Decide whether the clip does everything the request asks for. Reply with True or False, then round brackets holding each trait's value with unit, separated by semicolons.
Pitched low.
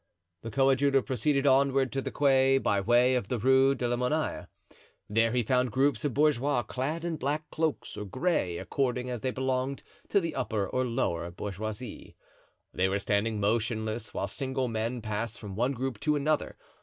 True (125 Hz)